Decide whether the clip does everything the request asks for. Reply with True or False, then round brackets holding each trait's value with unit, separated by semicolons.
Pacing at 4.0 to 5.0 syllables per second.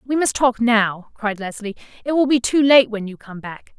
True (4.7 syllables/s)